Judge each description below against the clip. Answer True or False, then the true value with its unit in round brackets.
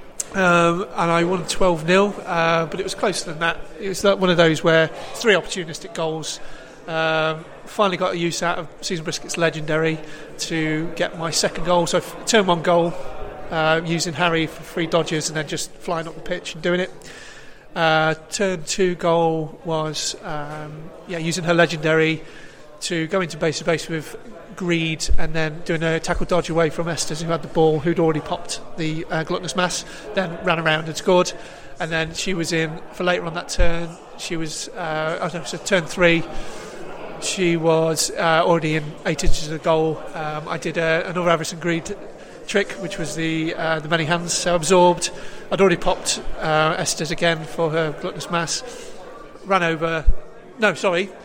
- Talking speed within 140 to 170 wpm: False (185 wpm)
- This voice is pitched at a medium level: True (165 Hz)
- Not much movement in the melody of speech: True (1.7 semitones)